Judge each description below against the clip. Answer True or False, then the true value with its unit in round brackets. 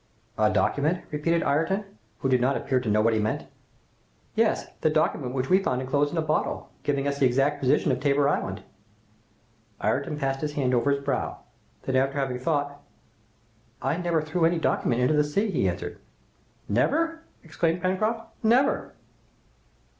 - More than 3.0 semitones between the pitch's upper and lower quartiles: True (4.2 semitones)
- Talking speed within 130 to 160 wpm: False (170 wpm)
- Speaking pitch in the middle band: True (145 Hz)